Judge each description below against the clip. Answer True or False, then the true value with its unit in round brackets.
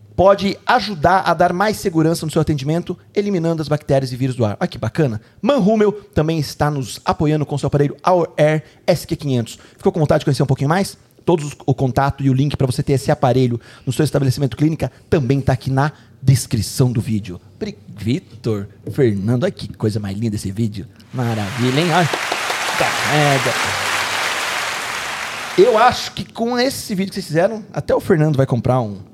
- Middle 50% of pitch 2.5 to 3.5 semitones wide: False (5.5 semitones)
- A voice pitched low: False (145 Hz)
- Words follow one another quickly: True (190 wpm)